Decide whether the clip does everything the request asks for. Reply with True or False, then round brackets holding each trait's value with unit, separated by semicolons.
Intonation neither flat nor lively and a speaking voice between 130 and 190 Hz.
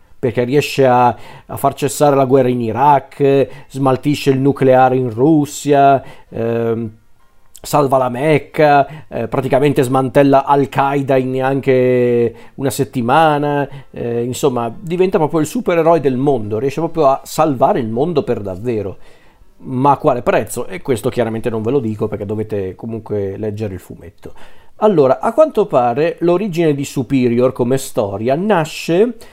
True (3.3 semitones; 135 Hz)